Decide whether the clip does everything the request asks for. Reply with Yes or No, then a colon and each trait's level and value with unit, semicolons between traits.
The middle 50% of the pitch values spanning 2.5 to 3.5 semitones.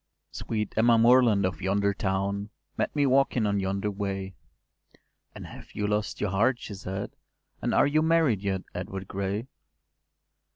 Yes: average, 3.1 semitones